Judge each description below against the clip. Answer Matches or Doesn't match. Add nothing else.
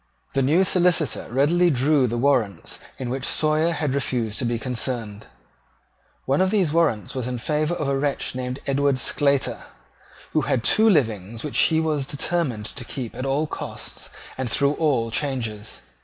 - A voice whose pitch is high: Doesn't match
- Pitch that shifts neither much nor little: Matches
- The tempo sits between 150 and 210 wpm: Matches